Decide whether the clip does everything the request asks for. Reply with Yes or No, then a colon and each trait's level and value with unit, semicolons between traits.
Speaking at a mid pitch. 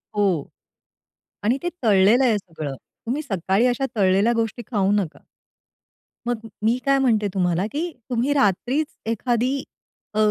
No: high, 225 Hz